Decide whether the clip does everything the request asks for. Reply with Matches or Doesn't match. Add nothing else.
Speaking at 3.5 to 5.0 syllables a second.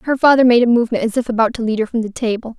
Doesn't match